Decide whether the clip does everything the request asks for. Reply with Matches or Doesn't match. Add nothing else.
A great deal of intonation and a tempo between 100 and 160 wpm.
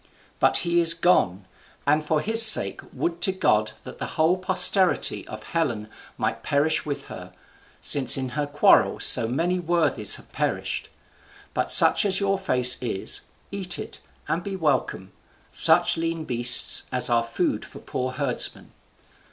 Matches